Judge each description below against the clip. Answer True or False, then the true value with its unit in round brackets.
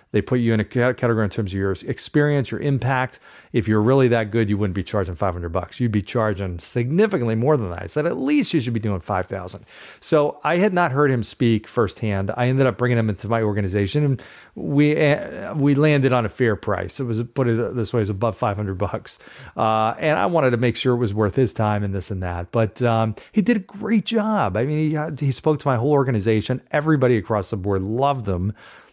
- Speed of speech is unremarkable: False (235 wpm)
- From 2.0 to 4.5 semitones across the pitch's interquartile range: False (5.2 semitones)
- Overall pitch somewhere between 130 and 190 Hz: False (120 Hz)